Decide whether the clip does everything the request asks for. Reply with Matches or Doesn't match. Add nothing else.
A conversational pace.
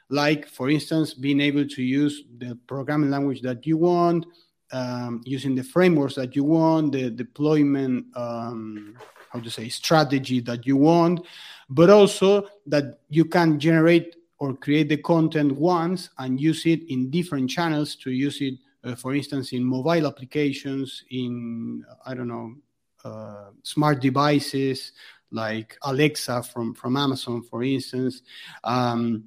Matches